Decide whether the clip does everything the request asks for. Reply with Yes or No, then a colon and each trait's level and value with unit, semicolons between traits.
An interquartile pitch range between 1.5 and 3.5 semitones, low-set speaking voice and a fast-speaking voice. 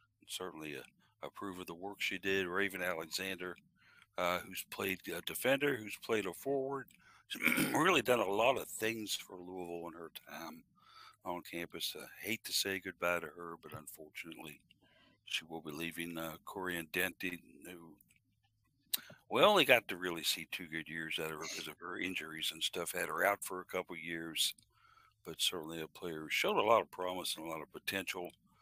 No: narrow, 2.5 semitones; very low, 90 Hz; average, 195 wpm